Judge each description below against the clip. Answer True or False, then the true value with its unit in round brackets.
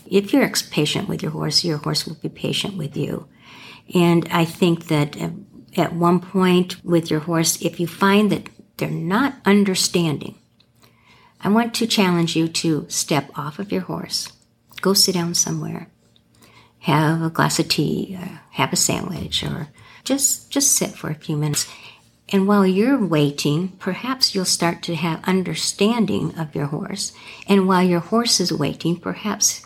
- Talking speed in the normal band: True (165 wpm)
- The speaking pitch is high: False (175 Hz)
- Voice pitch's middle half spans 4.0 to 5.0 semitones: False (3.5 semitones)